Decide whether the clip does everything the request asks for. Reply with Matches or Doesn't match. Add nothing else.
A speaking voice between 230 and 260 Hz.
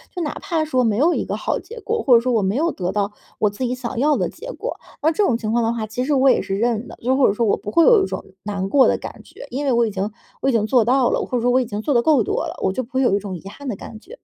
Matches